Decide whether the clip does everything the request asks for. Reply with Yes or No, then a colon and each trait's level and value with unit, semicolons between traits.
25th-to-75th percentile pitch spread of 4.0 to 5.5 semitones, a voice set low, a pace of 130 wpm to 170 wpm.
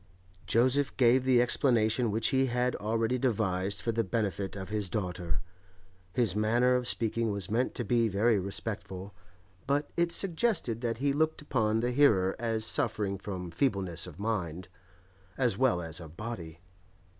Yes: average, 4.4 semitones; low, 110 Hz; average, 155 wpm